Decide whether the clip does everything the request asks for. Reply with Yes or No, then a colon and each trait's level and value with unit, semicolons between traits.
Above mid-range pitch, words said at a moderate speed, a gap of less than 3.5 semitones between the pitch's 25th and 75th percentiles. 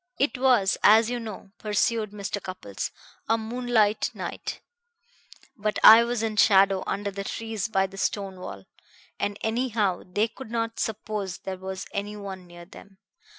Yes: high, 210 Hz; average, 155 wpm; average, 2.7 semitones